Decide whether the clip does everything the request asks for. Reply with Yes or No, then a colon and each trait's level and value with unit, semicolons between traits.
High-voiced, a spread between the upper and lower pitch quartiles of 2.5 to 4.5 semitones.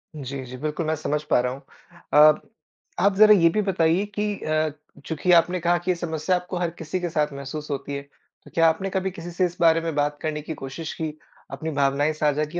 No: medium, 160 Hz; average, 2.9 semitones